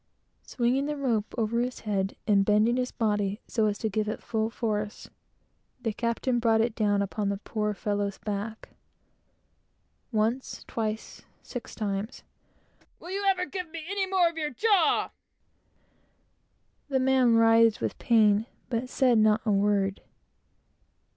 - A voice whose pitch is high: Yes, high, 225 Hz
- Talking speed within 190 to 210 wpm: No, average, 145 wpm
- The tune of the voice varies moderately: Yes, average, 3.4 semitones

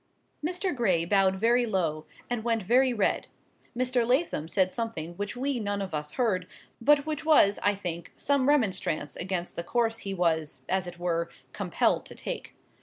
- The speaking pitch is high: Yes, high, 205 Hz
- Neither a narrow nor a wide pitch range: No, wide, 5.8 semitones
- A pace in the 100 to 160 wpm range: No, average, 175 wpm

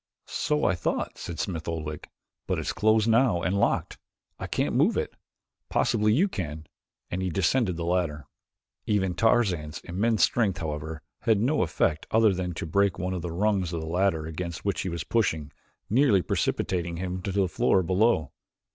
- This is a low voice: Yes, very low, 90 Hz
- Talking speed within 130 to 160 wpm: No, average, 175 wpm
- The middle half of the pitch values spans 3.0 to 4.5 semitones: Yes, average, 4.2 semitones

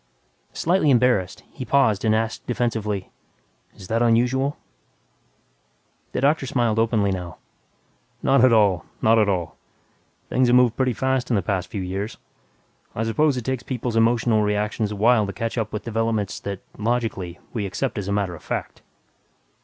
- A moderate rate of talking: Yes, average, 160 wpm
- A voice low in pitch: Yes, low, 115 Hz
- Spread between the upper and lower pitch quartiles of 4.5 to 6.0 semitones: No, average, 3.4 semitones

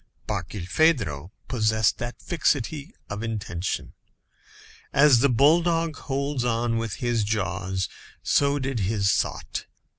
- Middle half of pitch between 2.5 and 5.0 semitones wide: No, wide, 5.6 semitones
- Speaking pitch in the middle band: No, low, 115 Hz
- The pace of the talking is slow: Yes, slow, 110 wpm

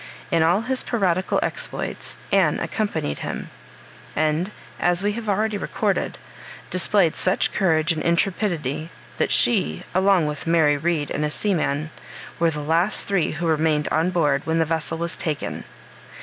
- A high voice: No, medium, 165 Hz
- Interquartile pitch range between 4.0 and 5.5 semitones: No, average, 3.5 semitones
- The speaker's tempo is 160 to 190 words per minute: No, average, 150 wpm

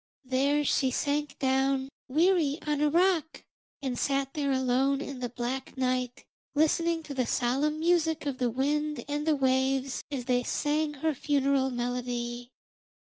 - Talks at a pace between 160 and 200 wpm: No, average, 150 wpm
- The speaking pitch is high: Yes, very high, 275 Hz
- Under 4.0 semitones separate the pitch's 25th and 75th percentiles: Yes, average, 2.7 semitones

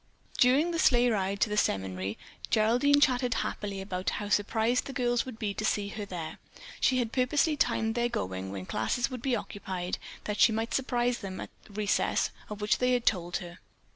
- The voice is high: Yes, high, 220 Hz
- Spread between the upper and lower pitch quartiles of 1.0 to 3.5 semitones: No, average, 4.3 semitones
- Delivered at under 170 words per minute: No, average, 200 wpm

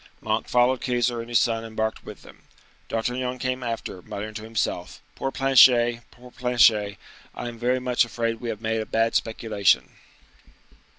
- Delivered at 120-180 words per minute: Yes, average, 160 wpm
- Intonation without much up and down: Yes, narrow, 1.8 semitones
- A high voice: No, low, 115 Hz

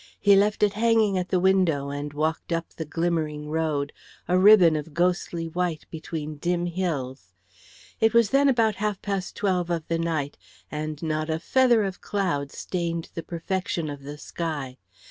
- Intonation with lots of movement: No, average, 3.7 semitones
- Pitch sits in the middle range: Yes, medium, 170 Hz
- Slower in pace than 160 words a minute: No, average, 170 wpm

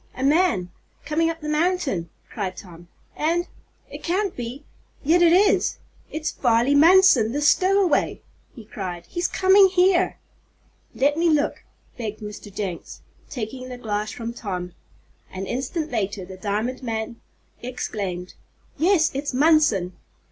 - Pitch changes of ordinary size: No, wide, 8.0 semitones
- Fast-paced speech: No, slow, 135 wpm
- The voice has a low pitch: No, very high, 255 Hz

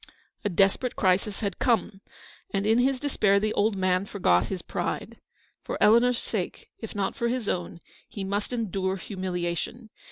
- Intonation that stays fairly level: No, average, 3.2 semitones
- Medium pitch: No, high, 200 Hz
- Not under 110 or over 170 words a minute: Yes, average, 160 wpm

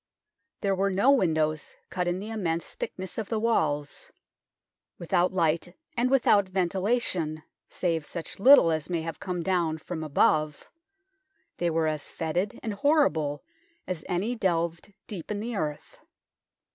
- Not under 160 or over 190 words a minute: No, average, 145 wpm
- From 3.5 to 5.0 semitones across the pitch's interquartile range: Yes, average, 4.1 semitones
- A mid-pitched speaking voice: Yes, medium, 180 Hz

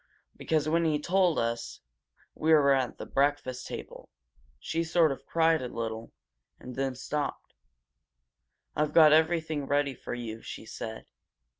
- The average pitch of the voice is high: No, medium, 145 Hz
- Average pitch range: Yes, average, 4.1 semitones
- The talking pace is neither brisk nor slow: Yes, average, 150 wpm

